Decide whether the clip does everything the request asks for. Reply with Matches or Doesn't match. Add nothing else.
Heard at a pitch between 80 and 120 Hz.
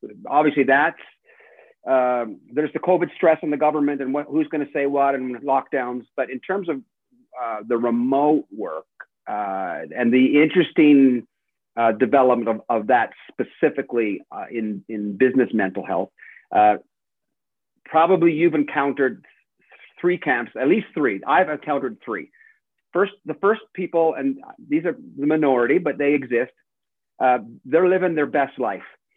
Doesn't match